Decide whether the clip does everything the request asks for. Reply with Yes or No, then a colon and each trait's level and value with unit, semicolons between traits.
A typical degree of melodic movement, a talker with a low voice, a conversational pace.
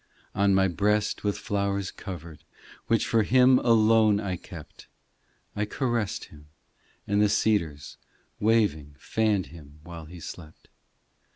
No: average, 4.2 semitones; low, 100 Hz; slow, 125 wpm